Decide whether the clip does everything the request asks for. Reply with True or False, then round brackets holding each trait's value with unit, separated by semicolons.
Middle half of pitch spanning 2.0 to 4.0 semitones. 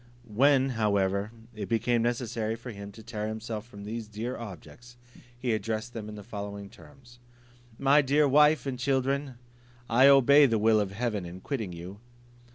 True (3.7 semitones)